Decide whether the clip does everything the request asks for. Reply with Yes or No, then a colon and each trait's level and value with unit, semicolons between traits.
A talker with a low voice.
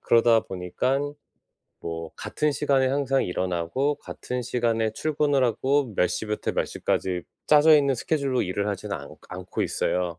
Yes: low, 120 Hz